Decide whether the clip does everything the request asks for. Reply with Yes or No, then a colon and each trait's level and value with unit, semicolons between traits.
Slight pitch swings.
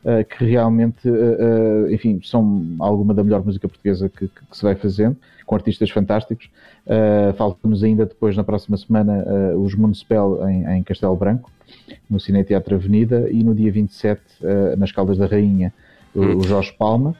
Yes: narrow, 1.9 semitones